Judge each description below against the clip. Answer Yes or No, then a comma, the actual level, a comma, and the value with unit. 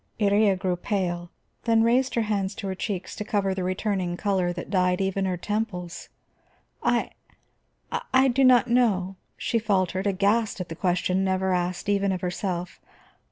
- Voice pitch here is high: Yes, high, 195 Hz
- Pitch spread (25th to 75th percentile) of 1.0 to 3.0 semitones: Yes, narrow, 2.6 semitones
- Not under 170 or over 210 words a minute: No, average, 160 wpm